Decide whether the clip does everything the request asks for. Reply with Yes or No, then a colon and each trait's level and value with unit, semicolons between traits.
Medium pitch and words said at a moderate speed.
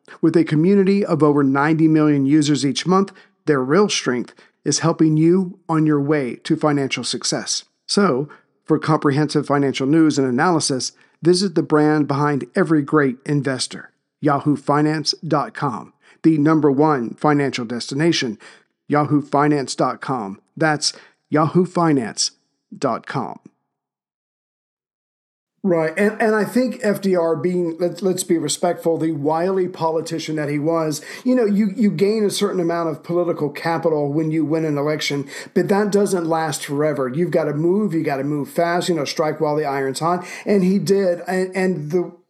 Yes: medium, 160 Hz; average, 150 wpm